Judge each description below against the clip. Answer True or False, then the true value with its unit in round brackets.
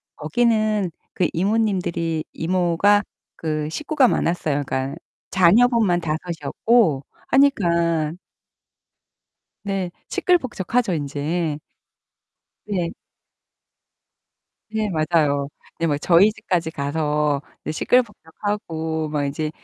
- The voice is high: False (170 Hz)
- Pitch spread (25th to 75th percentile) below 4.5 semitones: False (5.2 semitones)